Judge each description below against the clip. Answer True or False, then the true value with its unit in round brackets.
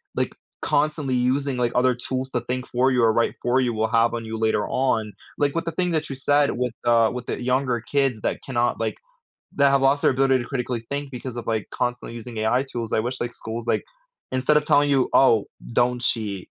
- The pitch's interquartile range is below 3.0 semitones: True (2.5 semitones)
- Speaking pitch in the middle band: False (125 Hz)